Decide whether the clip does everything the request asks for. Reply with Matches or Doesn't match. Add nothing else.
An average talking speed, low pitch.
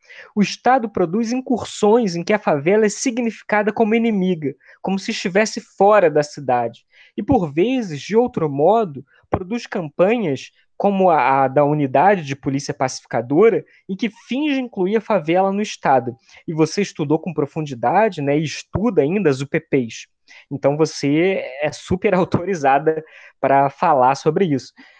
Doesn't match